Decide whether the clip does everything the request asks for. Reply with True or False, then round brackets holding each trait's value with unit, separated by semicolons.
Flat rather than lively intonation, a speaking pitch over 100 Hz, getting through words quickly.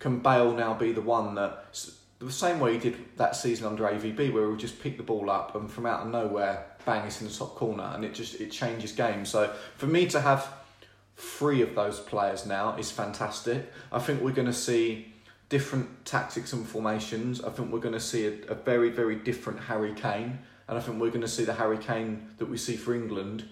True (2.3 semitones; 115 Hz; 230 wpm)